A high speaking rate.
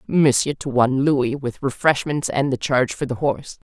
No: average, 195 wpm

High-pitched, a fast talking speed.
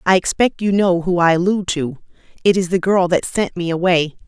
No: medium, 180 Hz; fast, 225 wpm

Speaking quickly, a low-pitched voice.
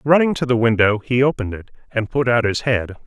Yes: fast, 235 wpm; low, 120 Hz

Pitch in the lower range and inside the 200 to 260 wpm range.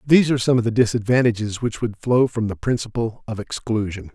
Yes: low, 115 Hz; fast, 205 wpm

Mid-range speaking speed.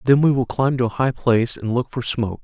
No: fast, 295 wpm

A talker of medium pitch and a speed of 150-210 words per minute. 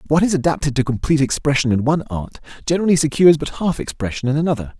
Yes: medium, 145 Hz; average, 200 wpm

